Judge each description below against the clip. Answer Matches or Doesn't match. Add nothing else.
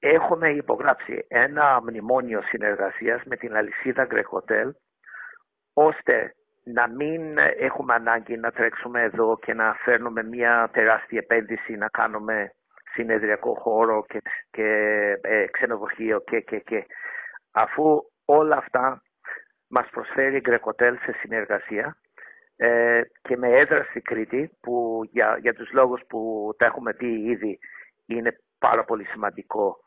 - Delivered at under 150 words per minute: Matches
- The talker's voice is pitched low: Matches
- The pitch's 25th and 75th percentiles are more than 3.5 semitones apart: Matches